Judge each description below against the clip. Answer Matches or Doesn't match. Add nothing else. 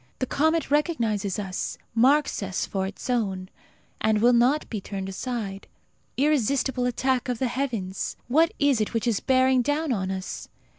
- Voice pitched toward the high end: Matches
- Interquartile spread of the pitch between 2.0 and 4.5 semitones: Doesn't match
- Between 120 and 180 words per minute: Matches